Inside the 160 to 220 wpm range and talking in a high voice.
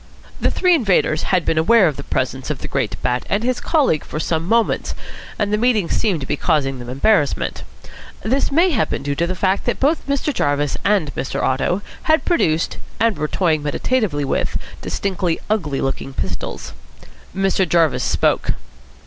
No: average, 180 wpm; medium, 175 Hz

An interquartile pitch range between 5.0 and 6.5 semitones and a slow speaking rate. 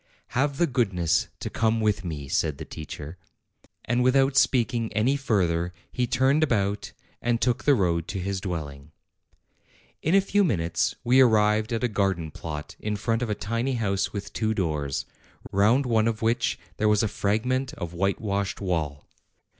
No: wide, 5.6 semitones; average, 170 wpm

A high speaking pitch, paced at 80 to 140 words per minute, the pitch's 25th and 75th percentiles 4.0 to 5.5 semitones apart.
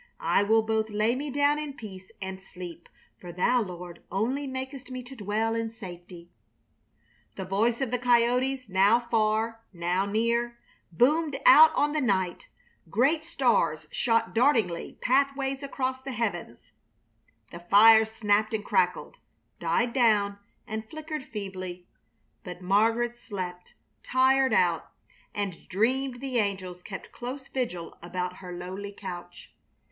Yes: high, 220 Hz; slow, 135 wpm; average, 5.2 semitones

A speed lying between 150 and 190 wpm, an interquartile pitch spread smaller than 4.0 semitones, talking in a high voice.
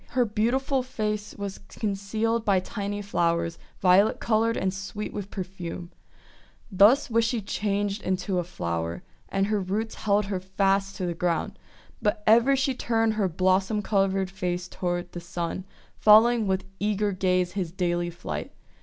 Yes: average, 165 wpm; average, 2.8 semitones; high, 195 Hz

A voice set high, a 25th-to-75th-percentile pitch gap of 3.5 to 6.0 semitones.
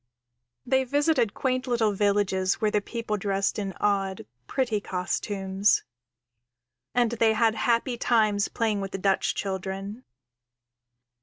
No: high, 210 Hz; average, 3.1 semitones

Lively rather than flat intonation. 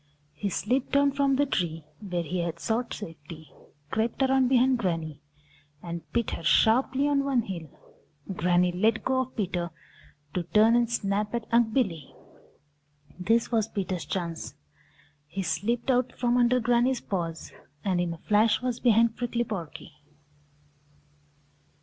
Yes: wide, 5.8 semitones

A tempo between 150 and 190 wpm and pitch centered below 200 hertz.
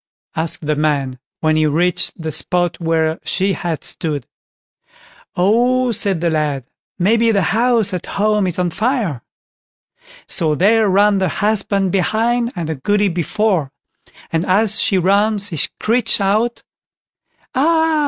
No: average, 140 wpm; high, 190 Hz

